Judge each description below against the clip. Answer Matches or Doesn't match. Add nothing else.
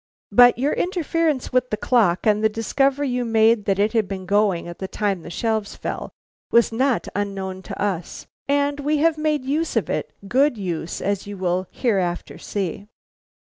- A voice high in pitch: Matches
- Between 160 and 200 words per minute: Matches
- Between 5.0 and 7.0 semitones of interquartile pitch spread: Matches